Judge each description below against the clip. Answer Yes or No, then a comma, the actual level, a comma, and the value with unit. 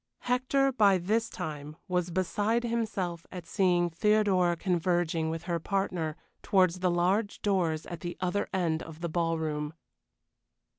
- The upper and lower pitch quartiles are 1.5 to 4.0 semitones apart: Yes, average, 3.4 semitones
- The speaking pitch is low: No, medium, 180 Hz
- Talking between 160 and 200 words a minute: No, average, 140 wpm